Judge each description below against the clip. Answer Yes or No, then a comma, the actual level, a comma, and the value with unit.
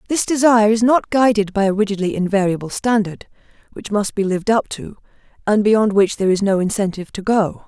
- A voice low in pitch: No, high, 205 Hz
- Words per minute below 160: No, average, 195 wpm